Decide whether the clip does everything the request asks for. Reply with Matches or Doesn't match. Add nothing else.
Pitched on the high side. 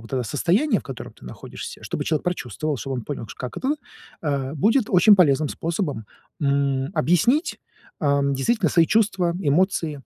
Doesn't match